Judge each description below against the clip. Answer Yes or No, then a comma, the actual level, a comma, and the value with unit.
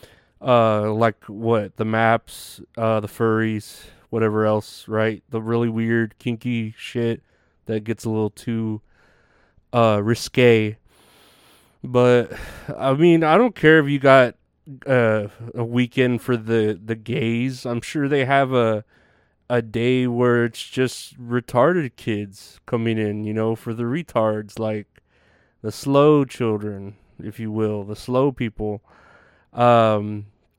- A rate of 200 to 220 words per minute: No, slow, 135 wpm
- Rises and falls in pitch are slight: Yes, narrow, 2.3 semitones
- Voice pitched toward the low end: Yes, low, 115 Hz